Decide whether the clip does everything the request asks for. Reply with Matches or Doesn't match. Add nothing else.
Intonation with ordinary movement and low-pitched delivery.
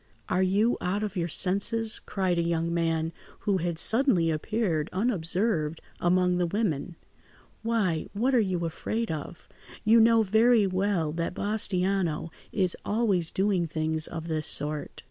Doesn't match